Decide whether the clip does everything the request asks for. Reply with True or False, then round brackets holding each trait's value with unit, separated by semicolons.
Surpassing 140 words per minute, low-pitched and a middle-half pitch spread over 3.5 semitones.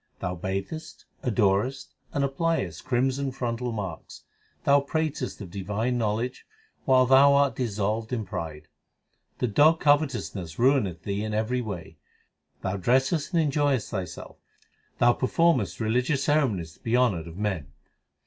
False (135 wpm; 120 Hz; 5.5 semitones)